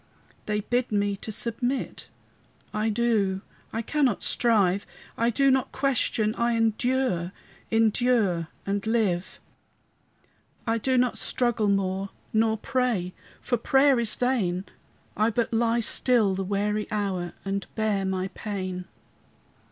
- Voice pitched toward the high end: Yes, high, 220 Hz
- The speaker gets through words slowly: Yes, slow, 125 wpm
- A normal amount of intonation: Yes, average, 3.3 semitones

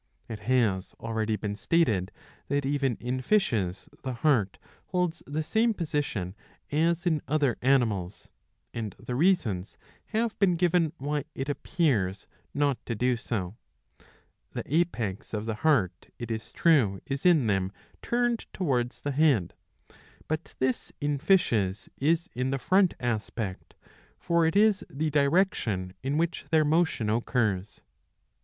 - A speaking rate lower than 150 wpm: Yes, average, 140 wpm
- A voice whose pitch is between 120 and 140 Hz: Yes, low, 135 Hz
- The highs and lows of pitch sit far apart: Yes, wide, 6.9 semitones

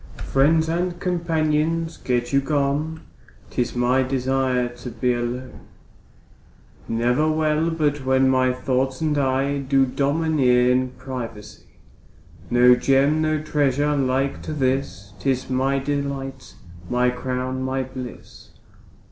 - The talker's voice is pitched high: No, low, 135 Hz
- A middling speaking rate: No, slow, 120 wpm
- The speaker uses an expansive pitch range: No, average, 2.8 semitones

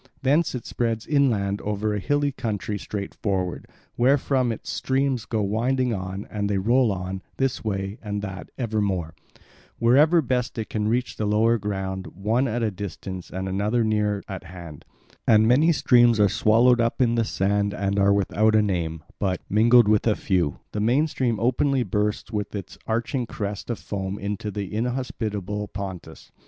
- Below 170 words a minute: No, average, 175 wpm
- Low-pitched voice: Yes, low, 105 Hz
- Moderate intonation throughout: Yes, average, 3.3 semitones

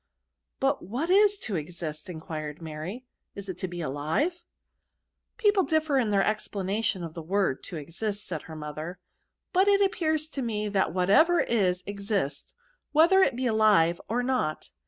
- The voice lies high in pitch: Yes, high, 200 Hz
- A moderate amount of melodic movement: No, wide, 8.5 semitones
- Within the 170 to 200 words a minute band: Yes, average, 180 wpm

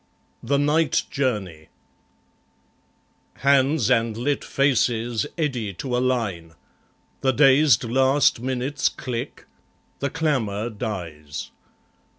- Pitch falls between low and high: No, low, 125 Hz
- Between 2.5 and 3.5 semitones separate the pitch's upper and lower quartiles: No, average, 4.2 semitones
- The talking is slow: Yes, slow, 95 wpm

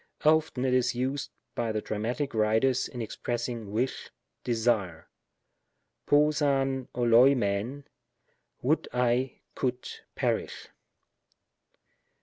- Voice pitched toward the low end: Yes, low, 125 Hz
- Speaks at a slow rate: Yes, slow, 100 wpm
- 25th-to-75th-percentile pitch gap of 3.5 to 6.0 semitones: No, average, 2.9 semitones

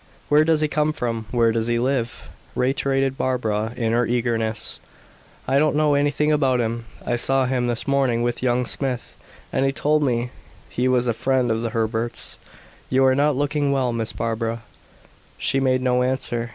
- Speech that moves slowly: No, average, 180 wpm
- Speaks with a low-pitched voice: Yes, low, 125 Hz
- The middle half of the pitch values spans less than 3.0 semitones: Yes, narrow, 2.6 semitones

